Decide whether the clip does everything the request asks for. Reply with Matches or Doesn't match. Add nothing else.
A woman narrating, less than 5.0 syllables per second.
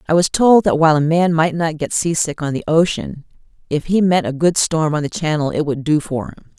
Doesn't match